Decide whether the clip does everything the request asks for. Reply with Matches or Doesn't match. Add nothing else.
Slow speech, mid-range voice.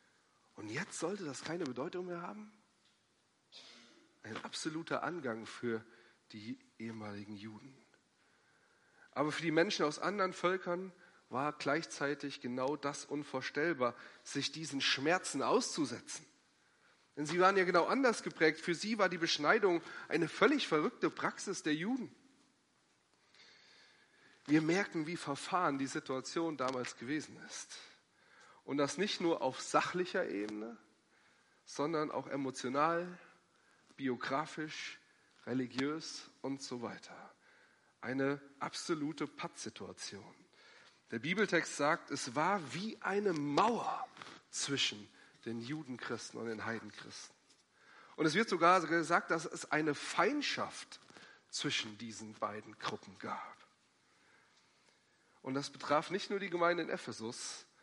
Matches